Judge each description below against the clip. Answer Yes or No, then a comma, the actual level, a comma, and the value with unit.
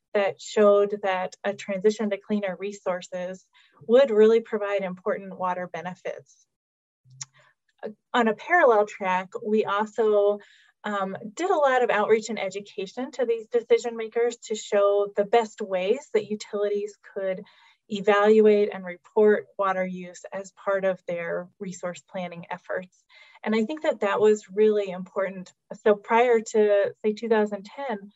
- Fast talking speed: No, average, 140 wpm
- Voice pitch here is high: Yes, high, 205 Hz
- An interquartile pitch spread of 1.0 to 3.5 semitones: Yes, narrow, 2.5 semitones